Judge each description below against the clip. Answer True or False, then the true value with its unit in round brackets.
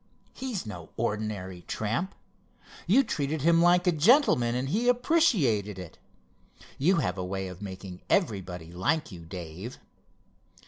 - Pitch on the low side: True (115 Hz)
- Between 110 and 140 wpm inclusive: True (135 wpm)